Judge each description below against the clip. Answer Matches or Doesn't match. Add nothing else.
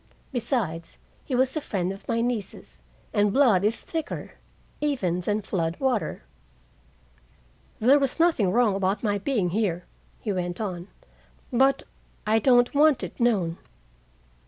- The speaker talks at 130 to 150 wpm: Matches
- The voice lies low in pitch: Doesn't match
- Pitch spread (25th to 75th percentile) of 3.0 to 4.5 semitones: Doesn't match